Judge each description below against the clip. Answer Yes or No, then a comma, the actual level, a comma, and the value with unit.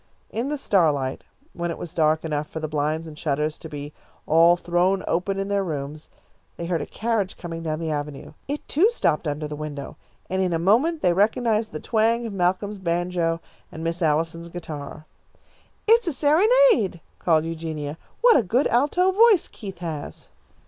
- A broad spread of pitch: Yes, wide, 5.8 semitones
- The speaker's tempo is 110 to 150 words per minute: No, average, 180 wpm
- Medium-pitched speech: Yes, medium, 170 Hz